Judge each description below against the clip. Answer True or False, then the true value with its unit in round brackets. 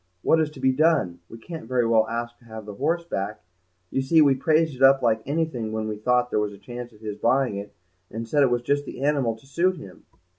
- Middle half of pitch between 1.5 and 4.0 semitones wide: False (4.5 semitones)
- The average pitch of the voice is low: True (125 Hz)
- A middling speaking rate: False (255 wpm)